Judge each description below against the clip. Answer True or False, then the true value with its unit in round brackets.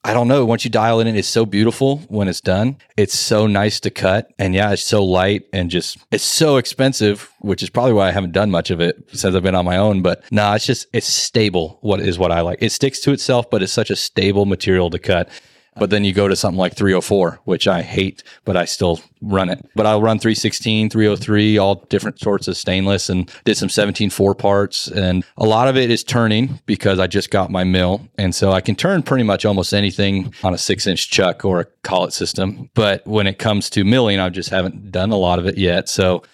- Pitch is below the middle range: True (100 Hz)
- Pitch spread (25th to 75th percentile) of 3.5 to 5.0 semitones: False (2.8 semitones)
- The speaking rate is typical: False (245 wpm)